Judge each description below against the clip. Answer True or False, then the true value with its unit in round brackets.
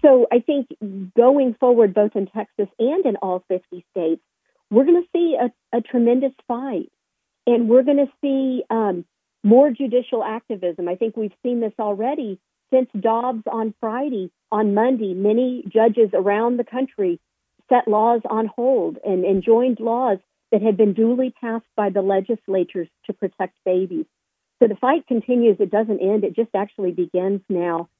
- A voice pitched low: False (225 Hz)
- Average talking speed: True (165 wpm)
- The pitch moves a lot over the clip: False (3.9 semitones)